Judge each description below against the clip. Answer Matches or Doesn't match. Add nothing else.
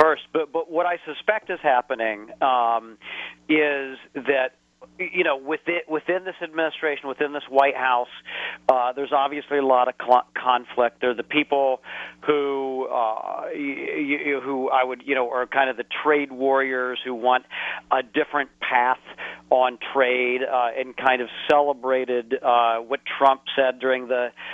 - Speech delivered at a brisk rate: Doesn't match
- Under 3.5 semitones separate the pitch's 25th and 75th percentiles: Matches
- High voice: Doesn't match